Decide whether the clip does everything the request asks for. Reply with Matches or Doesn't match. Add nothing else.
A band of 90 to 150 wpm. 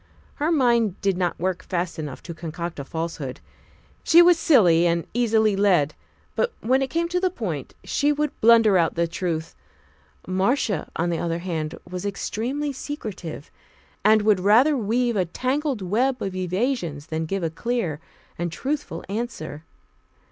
Doesn't match